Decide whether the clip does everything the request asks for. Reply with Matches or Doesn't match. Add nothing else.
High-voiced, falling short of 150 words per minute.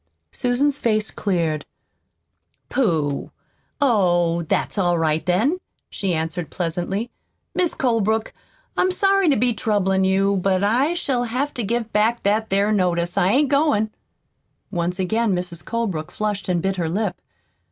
Matches